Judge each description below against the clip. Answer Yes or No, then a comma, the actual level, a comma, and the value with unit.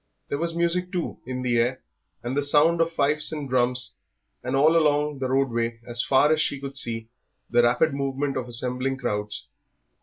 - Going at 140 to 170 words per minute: No, average, 180 wpm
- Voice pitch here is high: No, low, 135 Hz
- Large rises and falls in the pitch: No, average, 3.3 semitones